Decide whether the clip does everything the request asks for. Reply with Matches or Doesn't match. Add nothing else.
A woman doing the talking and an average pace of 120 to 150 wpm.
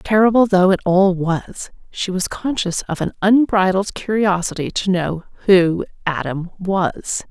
Matches